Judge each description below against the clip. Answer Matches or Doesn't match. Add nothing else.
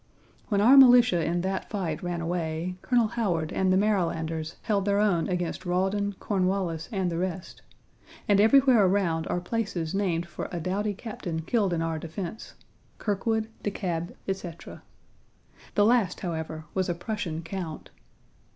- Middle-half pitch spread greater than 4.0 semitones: Doesn't match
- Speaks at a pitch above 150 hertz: Matches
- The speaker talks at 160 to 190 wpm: Doesn't match